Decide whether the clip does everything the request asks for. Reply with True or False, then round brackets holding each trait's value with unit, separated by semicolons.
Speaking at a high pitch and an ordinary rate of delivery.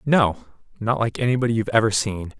False (110 Hz; 175 wpm)